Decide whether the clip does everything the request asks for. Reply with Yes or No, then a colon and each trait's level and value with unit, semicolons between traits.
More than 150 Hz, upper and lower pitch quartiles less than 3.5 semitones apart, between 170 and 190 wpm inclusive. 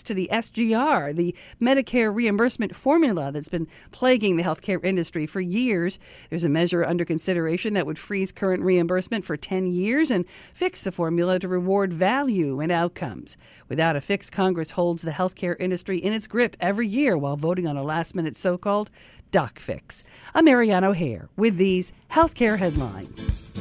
No: medium, 185 Hz; average, 4.2 semitones; average, 180 wpm